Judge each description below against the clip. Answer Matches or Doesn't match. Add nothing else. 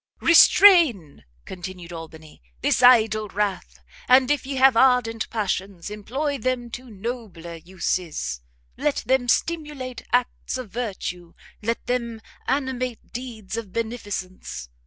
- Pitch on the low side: Doesn't match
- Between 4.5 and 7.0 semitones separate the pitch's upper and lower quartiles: Matches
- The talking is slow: Matches